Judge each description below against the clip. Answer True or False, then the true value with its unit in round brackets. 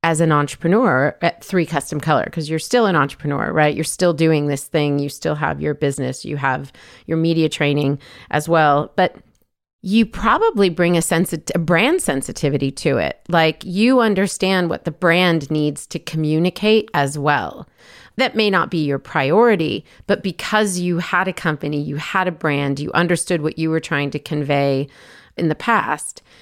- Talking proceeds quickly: False (180 wpm)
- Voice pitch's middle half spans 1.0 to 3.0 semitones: False (3.6 semitones)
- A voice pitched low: False (160 Hz)